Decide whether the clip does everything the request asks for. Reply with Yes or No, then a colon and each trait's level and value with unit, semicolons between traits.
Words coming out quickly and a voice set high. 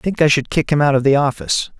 No: fast, 335 wpm; medium, 140 Hz